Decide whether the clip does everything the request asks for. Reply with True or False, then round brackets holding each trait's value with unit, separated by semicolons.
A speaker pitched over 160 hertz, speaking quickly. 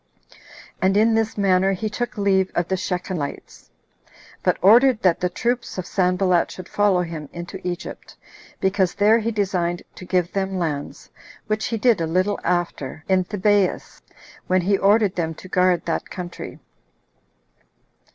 False (185 Hz; 150 wpm)